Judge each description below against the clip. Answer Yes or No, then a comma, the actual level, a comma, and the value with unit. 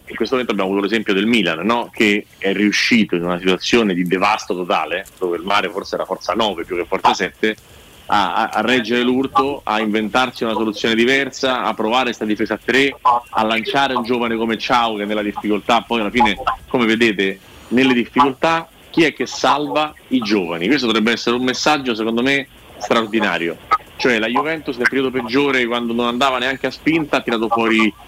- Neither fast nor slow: No, fast, 190 wpm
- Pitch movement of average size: Yes, average, 3.5 semitones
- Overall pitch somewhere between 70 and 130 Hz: Yes, low, 120 Hz